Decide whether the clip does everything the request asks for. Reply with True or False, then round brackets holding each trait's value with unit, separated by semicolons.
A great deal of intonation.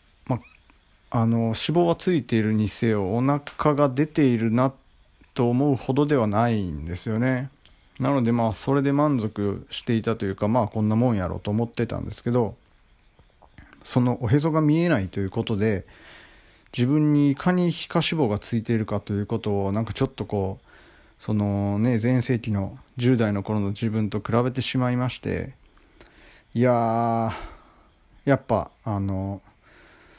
False (4.0 semitones)